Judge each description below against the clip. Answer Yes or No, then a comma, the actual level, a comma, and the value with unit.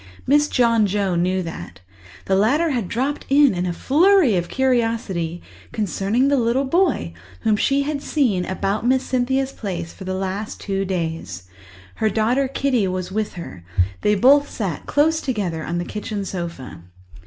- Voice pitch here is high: Yes, high, 215 Hz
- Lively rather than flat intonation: Yes, wide, 6.3 semitones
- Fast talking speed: No, average, 165 wpm